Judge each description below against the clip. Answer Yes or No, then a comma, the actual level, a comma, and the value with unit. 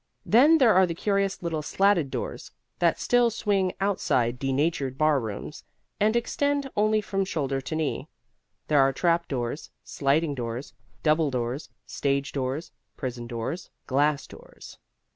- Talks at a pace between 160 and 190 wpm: No, average, 140 wpm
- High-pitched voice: No, medium, 155 Hz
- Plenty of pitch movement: Yes, wide, 6.6 semitones